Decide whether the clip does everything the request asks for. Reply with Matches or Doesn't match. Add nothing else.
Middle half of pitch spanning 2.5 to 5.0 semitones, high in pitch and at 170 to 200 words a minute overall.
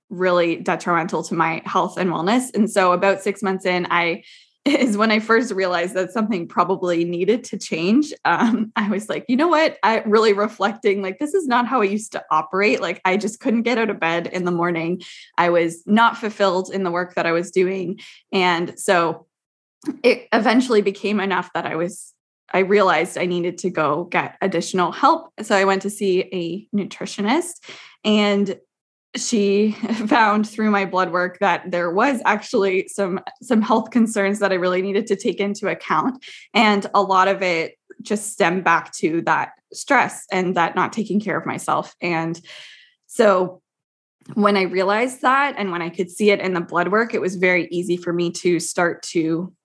Matches